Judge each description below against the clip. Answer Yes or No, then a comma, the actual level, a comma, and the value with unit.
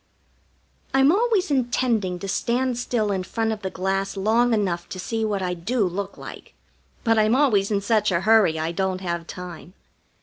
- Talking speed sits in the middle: Yes, average, 180 wpm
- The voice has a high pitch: Yes, high, 205 Hz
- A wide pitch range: No, average, 4.2 semitones